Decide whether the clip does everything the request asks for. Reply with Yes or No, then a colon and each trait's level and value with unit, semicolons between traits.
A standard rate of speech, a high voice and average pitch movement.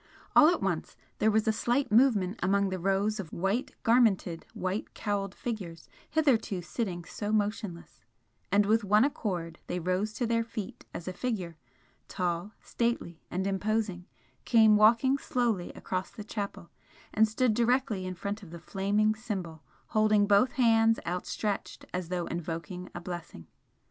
Yes: average, 155 wpm; high, 205 Hz; average, 3.7 semitones